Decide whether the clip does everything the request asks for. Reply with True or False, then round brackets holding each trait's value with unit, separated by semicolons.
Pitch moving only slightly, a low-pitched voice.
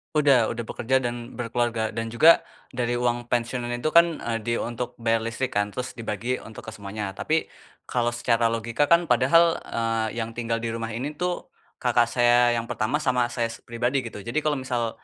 True (1.8 semitones; 120 Hz)